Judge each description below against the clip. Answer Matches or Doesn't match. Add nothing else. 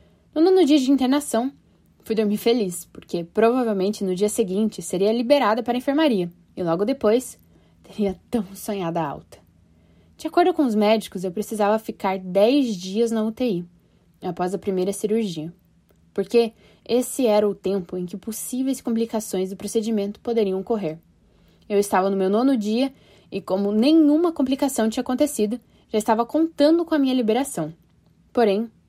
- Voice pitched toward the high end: Matches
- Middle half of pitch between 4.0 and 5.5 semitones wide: Matches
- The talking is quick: Doesn't match